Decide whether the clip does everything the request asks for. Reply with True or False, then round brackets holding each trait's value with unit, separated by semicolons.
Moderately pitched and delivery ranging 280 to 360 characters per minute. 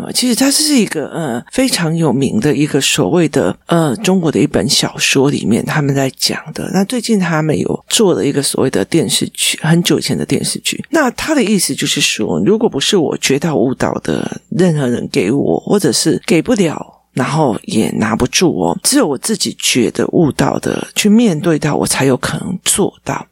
True (175 Hz; 290 characters per minute)